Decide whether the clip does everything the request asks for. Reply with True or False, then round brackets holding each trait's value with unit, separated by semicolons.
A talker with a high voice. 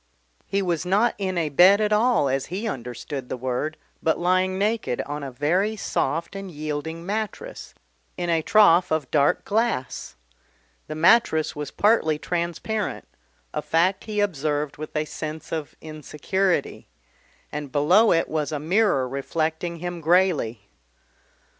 False (165 Hz)